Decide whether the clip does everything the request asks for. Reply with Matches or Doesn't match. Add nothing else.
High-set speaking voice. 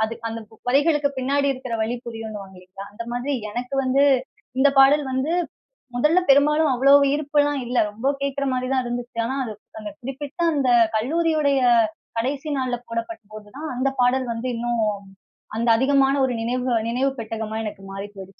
Matches